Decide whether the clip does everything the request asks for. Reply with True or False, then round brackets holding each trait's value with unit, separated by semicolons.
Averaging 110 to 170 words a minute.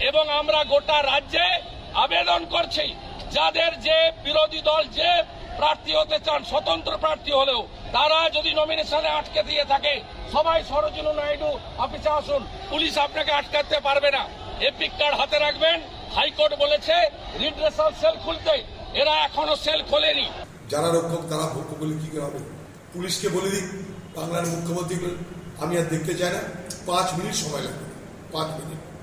True (120 wpm)